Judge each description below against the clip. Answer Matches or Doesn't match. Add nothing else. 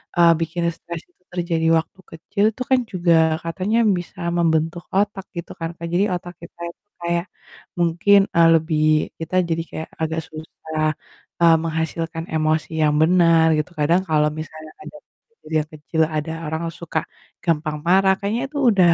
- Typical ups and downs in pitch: Doesn't match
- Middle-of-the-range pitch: Matches